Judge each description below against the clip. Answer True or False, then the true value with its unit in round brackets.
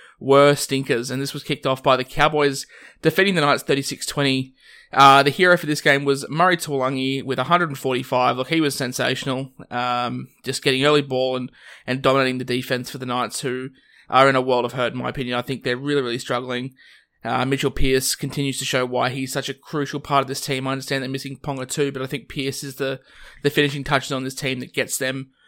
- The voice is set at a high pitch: False (135 Hz)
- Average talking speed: False (220 wpm)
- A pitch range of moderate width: False (1.6 semitones)